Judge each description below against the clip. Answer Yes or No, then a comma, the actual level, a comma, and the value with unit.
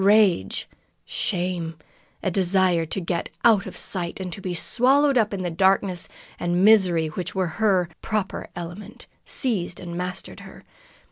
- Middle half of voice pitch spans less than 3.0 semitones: Yes, narrow, 2.5 semitones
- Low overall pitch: No, medium, 185 Hz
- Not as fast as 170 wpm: Yes, average, 145 wpm